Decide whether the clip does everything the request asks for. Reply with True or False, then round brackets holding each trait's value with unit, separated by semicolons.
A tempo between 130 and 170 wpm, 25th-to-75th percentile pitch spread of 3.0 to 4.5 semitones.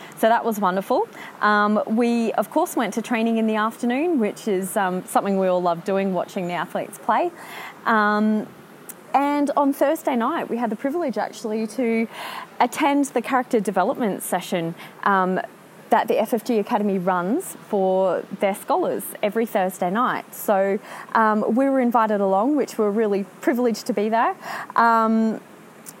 True (160 wpm; 4.0 semitones)